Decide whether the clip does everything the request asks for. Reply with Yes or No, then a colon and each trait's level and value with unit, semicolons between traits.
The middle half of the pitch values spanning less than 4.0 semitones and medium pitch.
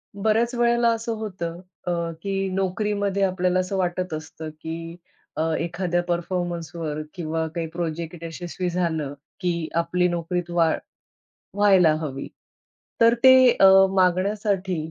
Yes: average, 2.7 semitones; medium, 180 Hz